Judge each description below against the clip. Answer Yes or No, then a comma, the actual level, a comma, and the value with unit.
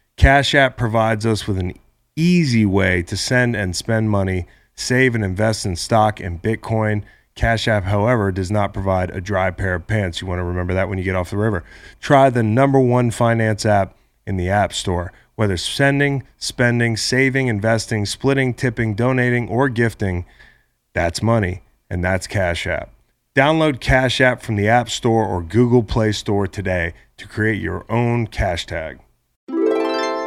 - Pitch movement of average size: Yes, average, 4.1 semitones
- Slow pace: No, average, 170 wpm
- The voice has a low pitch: Yes, low, 110 Hz